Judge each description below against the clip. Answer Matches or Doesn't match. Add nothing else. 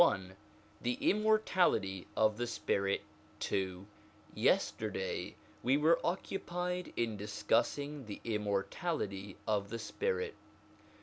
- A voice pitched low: Matches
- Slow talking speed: Matches